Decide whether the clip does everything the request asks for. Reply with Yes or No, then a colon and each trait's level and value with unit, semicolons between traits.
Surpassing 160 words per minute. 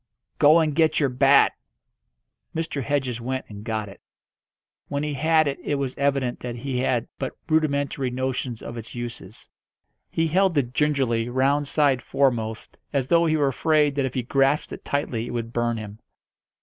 Yes: average, 175 wpm